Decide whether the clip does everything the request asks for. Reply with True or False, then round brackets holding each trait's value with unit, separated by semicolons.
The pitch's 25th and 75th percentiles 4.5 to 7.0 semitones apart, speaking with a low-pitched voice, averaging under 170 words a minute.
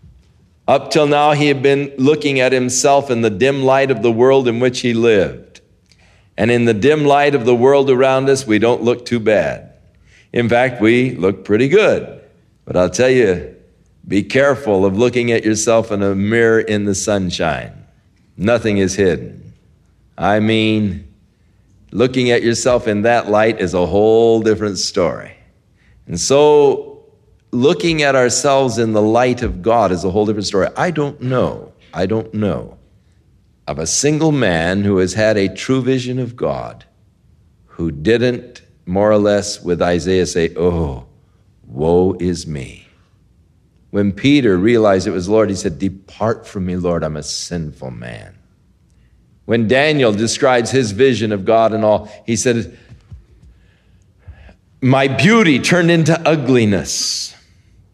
True (4.9 semitones; 110 Hz; 155 wpm)